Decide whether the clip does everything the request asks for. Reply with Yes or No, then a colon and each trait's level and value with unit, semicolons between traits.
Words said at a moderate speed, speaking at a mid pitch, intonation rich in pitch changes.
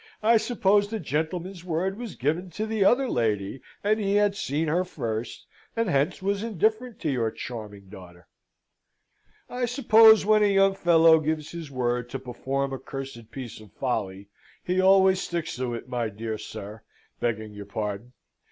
Yes: average, 170 wpm; medium, 155 Hz; wide, 8.9 semitones